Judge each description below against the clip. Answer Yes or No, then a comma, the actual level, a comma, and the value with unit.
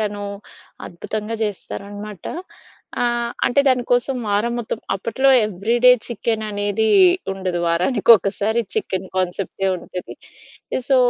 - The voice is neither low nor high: No, high, 210 Hz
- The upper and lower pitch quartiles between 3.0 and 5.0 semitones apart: Yes, average, 3.5 semitones